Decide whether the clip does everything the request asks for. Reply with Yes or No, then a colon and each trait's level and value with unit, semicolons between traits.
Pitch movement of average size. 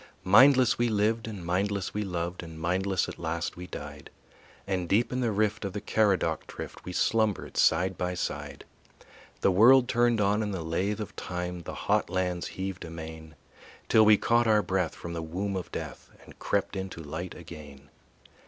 Yes: average, 3.6 semitones